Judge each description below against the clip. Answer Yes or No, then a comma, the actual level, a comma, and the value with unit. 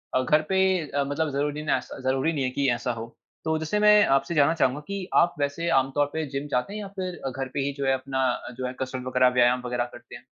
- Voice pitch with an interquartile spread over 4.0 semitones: No, average, 3.7 semitones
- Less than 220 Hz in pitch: Yes, medium, 140 Hz